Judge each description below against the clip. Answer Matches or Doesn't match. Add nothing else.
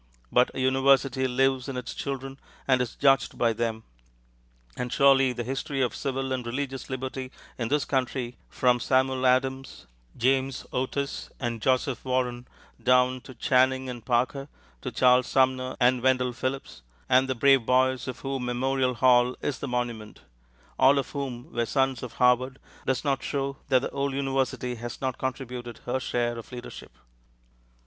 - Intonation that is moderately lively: Doesn't match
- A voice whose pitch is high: Doesn't match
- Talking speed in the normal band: Matches